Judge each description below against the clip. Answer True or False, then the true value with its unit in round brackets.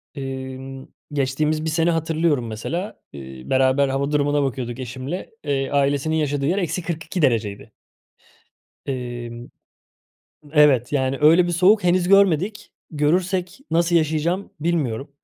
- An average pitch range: True (4.3 semitones)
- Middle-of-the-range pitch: True (145 Hz)